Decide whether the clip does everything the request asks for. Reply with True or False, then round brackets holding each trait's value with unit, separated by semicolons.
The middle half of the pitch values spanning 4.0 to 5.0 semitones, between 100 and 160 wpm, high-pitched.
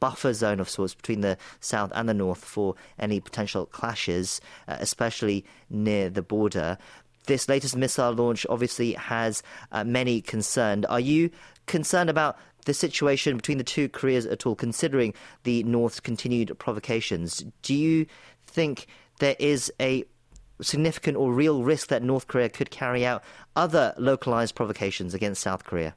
False (4.4 semitones; 155 wpm; 120 Hz)